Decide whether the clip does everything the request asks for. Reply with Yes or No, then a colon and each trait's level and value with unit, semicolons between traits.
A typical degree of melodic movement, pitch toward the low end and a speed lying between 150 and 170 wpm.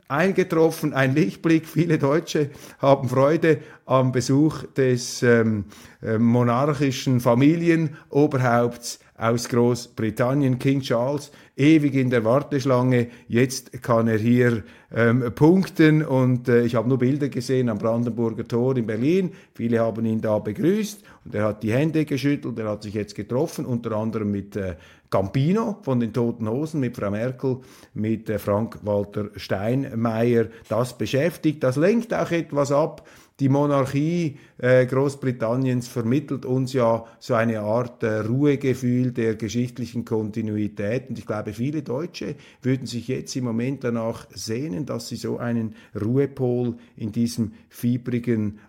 No: average, 3.6 semitones; low, 125 Hz; average, 140 wpm